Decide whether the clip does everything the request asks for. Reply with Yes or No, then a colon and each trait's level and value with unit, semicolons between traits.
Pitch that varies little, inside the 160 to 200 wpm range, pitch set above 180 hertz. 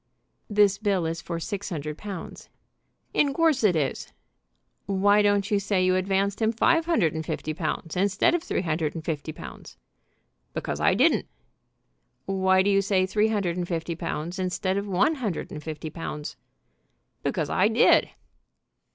No: average, 3.7 semitones; average, 165 wpm; high, 190 Hz